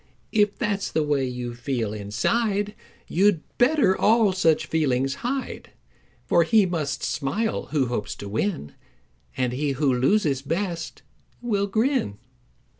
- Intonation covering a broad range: Yes, wide, 8.0 semitones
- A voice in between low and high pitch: Yes, medium, 160 Hz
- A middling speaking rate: No, slow, 130 wpm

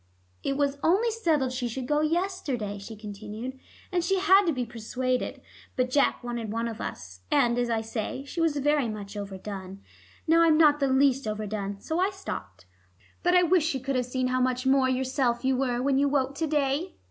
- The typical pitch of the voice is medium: No, very high, 260 Hz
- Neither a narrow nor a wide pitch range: Yes, average, 4.6 semitones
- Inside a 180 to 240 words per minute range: Yes, fast, 205 wpm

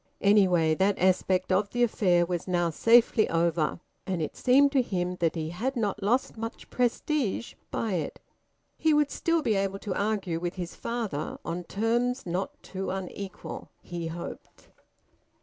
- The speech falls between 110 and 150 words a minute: No, average, 160 wpm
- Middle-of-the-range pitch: No, high, 195 Hz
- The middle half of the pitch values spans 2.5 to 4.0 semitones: No, average, 4.8 semitones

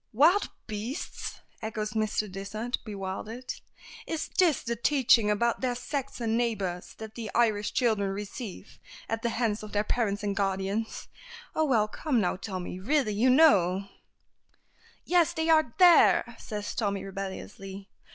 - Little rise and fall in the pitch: No, average, 3.6 semitones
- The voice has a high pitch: Yes, high, 220 Hz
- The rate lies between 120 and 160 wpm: Yes, average, 140 wpm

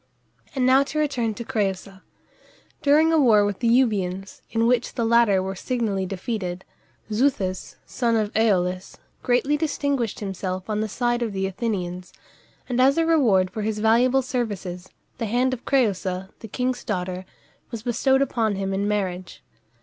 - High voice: Yes, high, 220 Hz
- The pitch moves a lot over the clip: No, average, 4.6 semitones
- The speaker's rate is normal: Yes, average, 160 wpm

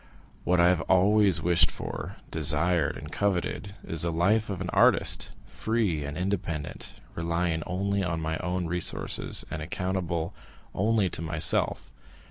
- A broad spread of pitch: No, average, 2.9 semitones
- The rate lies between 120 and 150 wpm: Yes, average, 140 wpm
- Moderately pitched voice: No, very low, 90 Hz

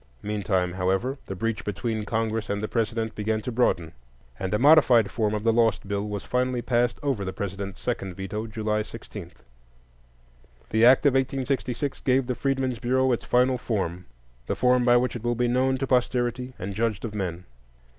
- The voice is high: No, low, 115 Hz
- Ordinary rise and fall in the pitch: Yes, average, 3.7 semitones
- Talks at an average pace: Yes, average, 180 wpm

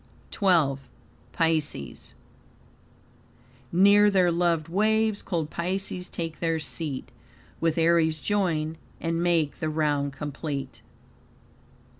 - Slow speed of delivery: Yes, slow, 95 wpm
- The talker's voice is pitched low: No, medium, 165 Hz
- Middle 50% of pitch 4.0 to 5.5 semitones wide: No, average, 2.7 semitones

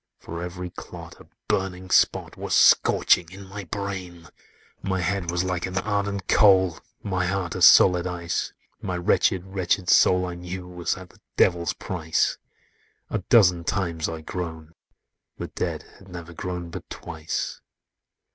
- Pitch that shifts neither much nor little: No, narrow, 1.7 semitones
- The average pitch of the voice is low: Yes, very low, 90 Hz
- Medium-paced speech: Yes, average, 150 wpm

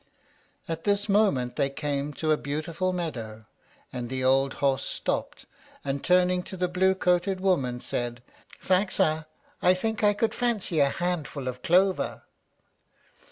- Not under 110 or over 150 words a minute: Yes, average, 145 wpm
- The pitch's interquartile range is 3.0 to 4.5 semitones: No, average, 5.3 semitones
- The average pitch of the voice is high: No, medium, 165 Hz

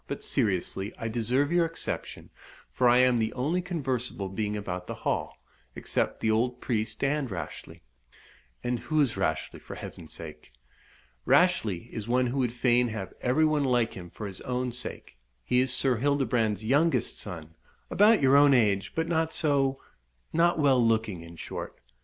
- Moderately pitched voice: No, low, 125 Hz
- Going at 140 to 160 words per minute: No, average, 170 wpm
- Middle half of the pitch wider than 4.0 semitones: Yes, average, 4.9 semitones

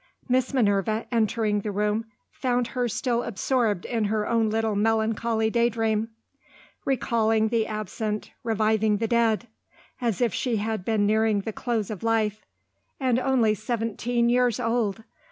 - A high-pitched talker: Yes, high, 225 Hz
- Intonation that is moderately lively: No, narrow, 1.7 semitones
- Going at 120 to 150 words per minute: Yes, average, 140 wpm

